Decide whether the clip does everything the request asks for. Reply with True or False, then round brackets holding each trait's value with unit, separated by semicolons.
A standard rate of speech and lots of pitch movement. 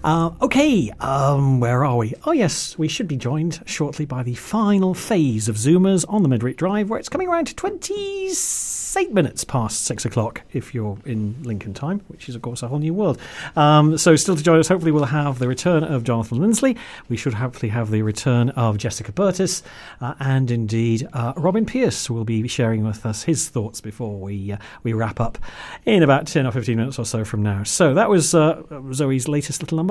False (215 wpm; 6.6 semitones)